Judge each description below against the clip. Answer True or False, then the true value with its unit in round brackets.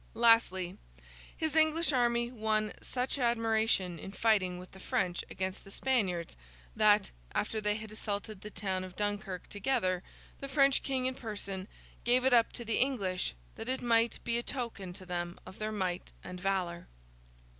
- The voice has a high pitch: True (215 Hz)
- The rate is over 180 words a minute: False (165 wpm)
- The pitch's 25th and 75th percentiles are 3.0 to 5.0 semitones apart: True (4.2 semitones)